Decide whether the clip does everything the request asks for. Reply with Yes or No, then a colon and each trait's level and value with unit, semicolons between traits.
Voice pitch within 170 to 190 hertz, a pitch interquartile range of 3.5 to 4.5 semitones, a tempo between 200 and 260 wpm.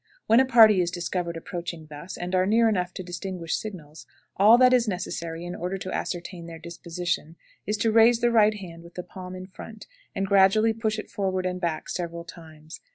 Yes: medium, 185 Hz; average, 3.8 semitones; fast, 205 wpm